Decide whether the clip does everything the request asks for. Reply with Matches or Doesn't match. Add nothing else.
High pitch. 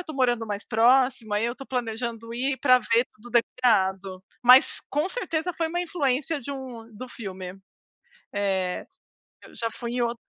Matches